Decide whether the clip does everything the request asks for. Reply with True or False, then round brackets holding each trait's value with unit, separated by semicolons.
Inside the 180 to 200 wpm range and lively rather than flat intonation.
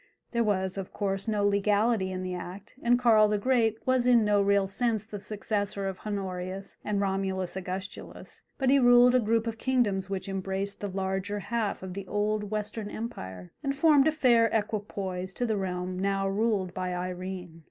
False (185 wpm; 2.9 semitones)